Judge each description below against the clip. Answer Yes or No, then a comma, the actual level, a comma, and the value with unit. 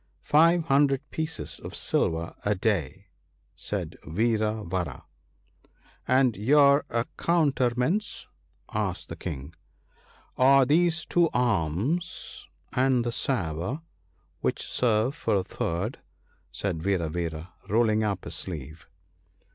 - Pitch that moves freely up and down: Yes, wide, 7.5 semitones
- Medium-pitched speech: No, low, 110 Hz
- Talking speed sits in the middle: No, slow, 120 wpm